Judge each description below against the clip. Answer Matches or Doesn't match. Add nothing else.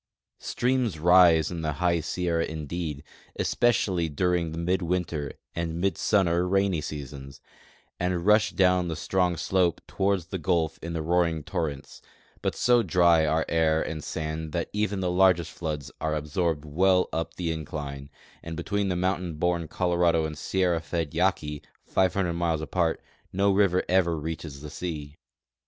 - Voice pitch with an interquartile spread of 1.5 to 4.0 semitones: Matches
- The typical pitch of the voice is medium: Doesn't match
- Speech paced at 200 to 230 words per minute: Doesn't match